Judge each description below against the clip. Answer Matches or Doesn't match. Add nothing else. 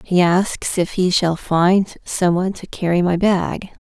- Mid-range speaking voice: Matches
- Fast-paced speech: Doesn't match